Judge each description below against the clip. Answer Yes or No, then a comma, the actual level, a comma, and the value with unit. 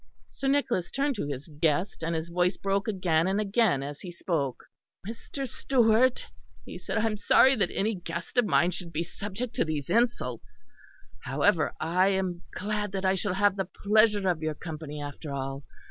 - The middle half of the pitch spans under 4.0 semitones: No, average, 4.9 semitones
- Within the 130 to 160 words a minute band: No, average, 185 wpm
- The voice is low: No, medium, 185 Hz